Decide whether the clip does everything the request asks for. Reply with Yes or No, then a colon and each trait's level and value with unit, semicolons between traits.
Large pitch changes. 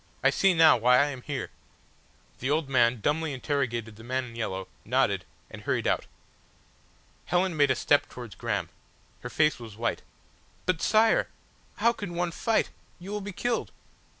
Yes: wide, 6.5 semitones